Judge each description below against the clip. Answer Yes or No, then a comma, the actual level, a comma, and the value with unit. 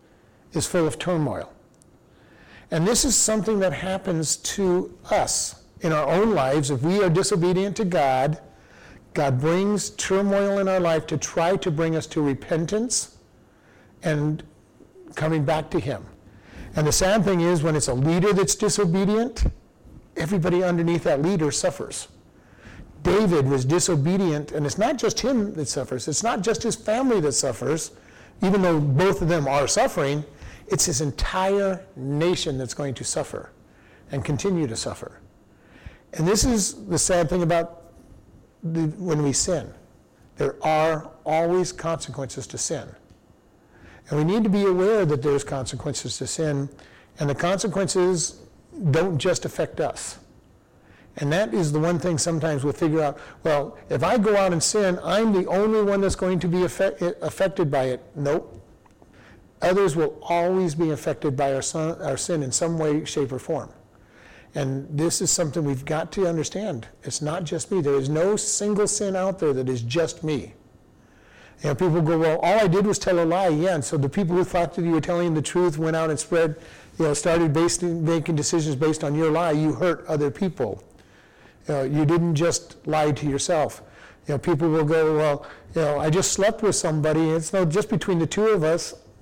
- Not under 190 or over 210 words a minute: No, average, 180 wpm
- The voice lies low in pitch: No, medium, 165 Hz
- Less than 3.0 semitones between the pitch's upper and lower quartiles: No, average, 4.2 semitones